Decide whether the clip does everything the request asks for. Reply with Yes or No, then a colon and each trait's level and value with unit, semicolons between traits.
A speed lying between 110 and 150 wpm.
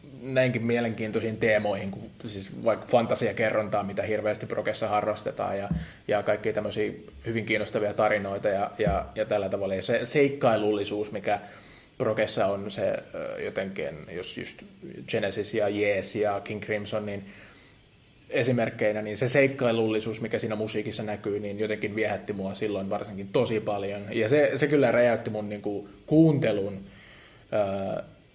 Yes: average, 140 wpm